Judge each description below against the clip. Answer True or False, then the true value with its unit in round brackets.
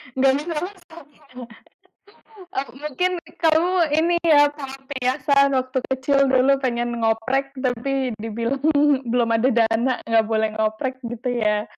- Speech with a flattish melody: False (3.7 semitones)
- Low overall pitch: False (260 Hz)